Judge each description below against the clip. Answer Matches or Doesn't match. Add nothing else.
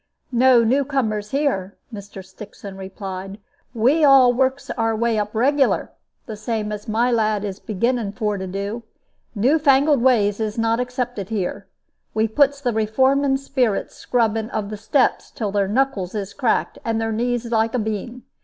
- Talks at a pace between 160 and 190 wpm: Matches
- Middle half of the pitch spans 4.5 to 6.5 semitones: Doesn't match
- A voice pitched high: Matches